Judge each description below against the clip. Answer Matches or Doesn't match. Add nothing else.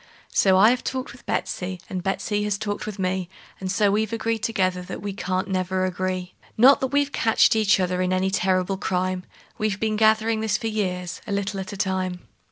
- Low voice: Doesn't match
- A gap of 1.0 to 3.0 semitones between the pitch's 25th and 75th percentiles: Matches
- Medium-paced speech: Doesn't match